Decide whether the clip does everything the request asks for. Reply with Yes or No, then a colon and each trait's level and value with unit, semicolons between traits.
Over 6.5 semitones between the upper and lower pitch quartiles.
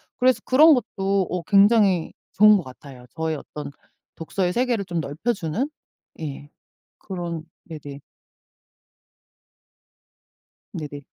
No: wide, 5.5 semitones